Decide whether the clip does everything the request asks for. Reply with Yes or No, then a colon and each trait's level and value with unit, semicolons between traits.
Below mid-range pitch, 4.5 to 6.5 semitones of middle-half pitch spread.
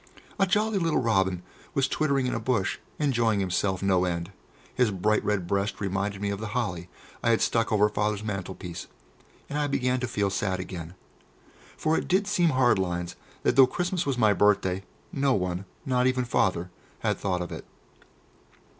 Yes: low, 105 Hz; wide, 5.4 semitones